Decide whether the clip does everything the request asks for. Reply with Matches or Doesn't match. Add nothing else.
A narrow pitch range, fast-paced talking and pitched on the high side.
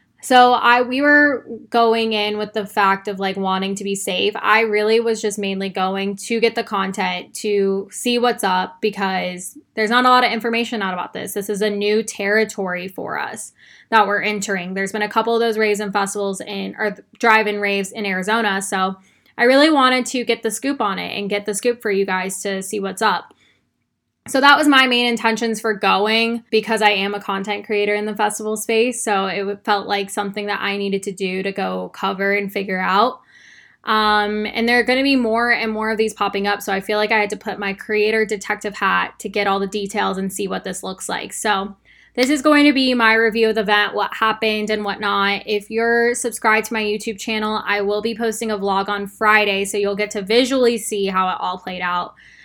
Matches